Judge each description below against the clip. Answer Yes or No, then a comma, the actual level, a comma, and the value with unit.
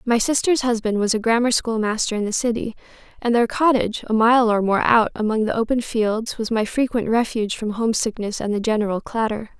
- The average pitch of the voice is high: Yes, high, 225 Hz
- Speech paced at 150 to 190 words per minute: No, fast, 205 wpm